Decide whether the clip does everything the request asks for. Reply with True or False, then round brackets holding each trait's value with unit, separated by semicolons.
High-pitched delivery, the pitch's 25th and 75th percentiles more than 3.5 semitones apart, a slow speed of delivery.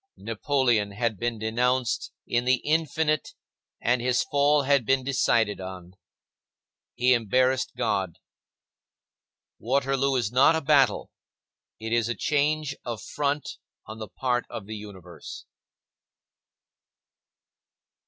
False (125 Hz; 3.9 semitones; 115 wpm)